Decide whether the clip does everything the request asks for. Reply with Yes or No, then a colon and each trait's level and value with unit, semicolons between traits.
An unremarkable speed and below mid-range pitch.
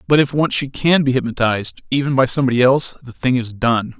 Yes: average, 195 wpm; low, 130 Hz